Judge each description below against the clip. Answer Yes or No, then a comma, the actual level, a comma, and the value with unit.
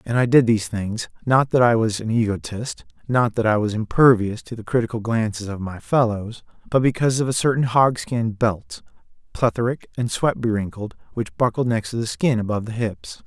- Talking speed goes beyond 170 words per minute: Yes, average, 190 wpm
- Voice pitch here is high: No, low, 115 Hz